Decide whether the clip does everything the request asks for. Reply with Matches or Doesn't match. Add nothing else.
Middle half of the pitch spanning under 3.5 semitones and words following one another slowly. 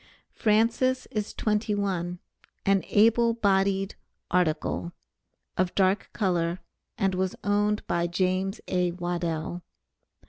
Matches